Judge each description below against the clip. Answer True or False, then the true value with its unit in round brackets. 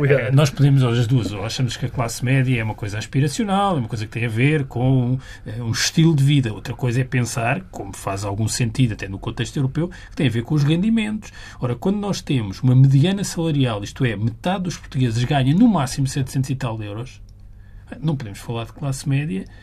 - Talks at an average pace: False (220 wpm)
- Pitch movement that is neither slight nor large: True (3.9 semitones)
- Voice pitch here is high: False (130 Hz)